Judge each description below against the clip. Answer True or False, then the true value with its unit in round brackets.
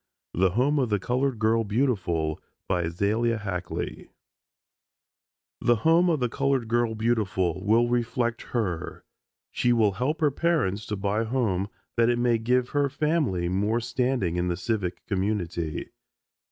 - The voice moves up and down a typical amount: True (4.6 semitones)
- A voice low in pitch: True (115 Hz)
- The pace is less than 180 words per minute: True (145 wpm)